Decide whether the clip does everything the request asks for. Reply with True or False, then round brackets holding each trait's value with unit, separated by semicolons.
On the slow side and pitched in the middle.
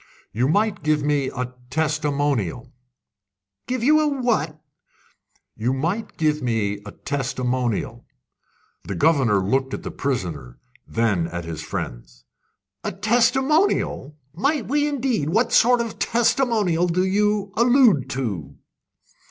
True (120 wpm; 150 Hz)